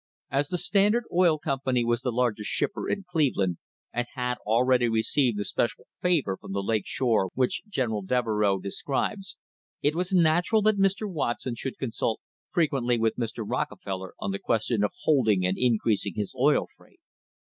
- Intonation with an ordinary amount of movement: No, wide, 6.2 semitones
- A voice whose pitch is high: No, low, 125 Hz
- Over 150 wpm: Yes, average, 170 wpm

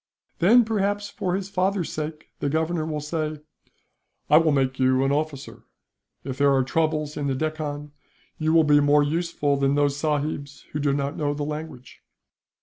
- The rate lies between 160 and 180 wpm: Yes, average, 175 wpm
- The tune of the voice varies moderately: No, narrow, 2.1 semitones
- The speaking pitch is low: No, medium, 150 Hz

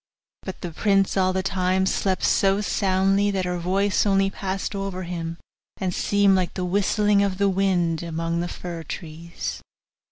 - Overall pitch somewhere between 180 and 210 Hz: Yes, high, 190 Hz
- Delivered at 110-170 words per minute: Yes, average, 165 wpm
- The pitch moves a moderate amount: No, narrow, 1.9 semitones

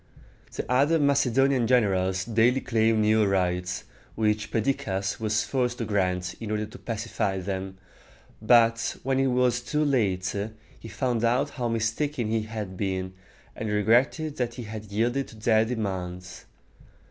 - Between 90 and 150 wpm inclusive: Yes, average, 145 wpm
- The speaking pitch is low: Yes, low, 110 Hz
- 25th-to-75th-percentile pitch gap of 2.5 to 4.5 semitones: Yes, average, 3.8 semitones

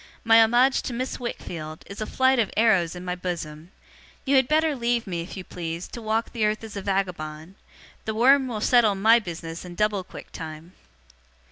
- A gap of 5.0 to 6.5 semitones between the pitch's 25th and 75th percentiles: Yes, average, 5.3 semitones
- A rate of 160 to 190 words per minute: No, average, 200 wpm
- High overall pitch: Yes, high, 210 Hz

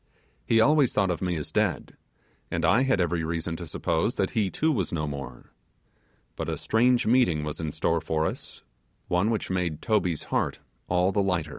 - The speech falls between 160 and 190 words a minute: Yes, average, 185 wpm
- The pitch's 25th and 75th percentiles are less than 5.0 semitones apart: No, wide, 5.4 semitones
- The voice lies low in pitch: Yes, very low, 90 Hz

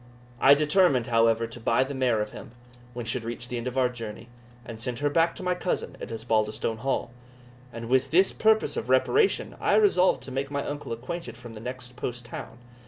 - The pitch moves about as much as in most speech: Yes, average, 3.6 semitones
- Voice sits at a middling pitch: No, low, 125 Hz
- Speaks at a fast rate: Yes, fast, 215 wpm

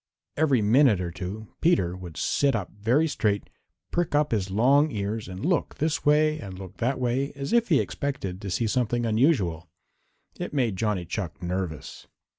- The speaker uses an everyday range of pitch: No, wide, 7.0 semitones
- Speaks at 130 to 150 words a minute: No, average, 175 wpm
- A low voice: Yes, low, 110 Hz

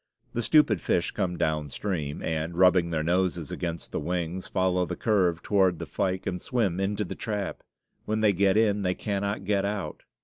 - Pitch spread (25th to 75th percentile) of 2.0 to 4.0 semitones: Yes, average, 3.0 semitones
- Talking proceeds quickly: No, average, 180 wpm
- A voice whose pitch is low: Yes, very low, 95 Hz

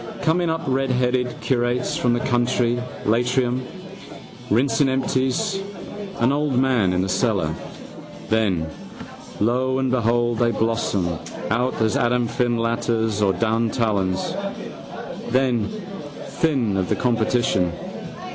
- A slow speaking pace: Yes, slow, 110 wpm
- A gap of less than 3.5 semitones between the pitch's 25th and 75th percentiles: Yes, average, 2.8 semitones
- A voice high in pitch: No, low, 120 Hz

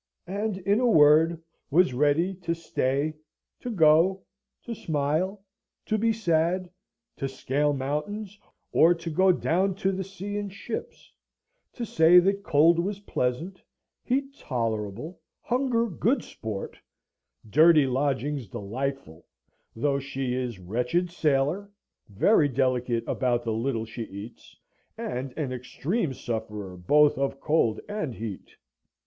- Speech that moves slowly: Yes, slow, 130 wpm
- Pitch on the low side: No, medium, 150 Hz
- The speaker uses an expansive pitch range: Yes, wide, 6.9 semitones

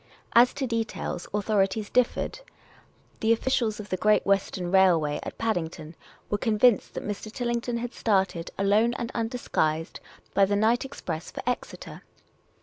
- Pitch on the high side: Yes, high, 210 Hz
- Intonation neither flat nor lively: Yes, average, 3.6 semitones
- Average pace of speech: Yes, average, 145 wpm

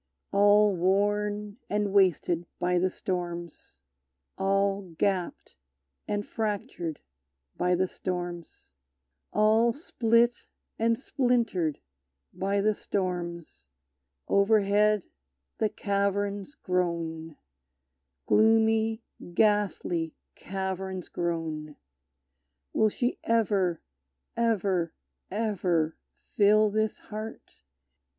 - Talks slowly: Yes, slow, 80 wpm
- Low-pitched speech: No, high, 200 Hz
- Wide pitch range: No, average, 3.2 semitones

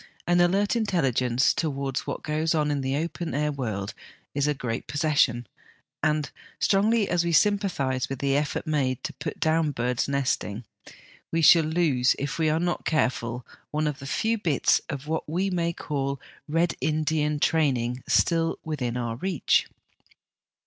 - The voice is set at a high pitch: No, medium, 150 Hz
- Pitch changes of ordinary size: Yes, average, 3.9 semitones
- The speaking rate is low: No, average, 160 wpm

